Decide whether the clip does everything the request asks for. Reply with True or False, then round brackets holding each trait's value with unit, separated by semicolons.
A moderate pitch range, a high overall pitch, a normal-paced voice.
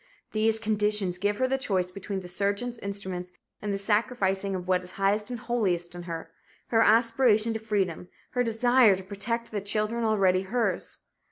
True (3.2 semitones; 205 Hz; 175 wpm)